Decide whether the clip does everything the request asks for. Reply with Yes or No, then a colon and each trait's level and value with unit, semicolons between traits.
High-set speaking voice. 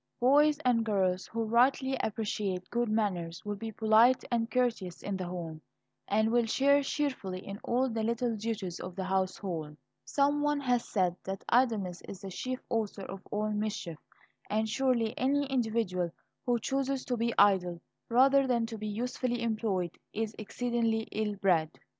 Yes: high, 220 Hz